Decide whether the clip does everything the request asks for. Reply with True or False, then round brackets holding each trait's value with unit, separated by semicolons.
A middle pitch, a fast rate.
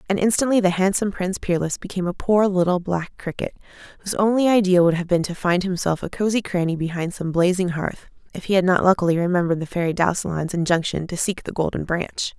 True (180 Hz; 210 wpm)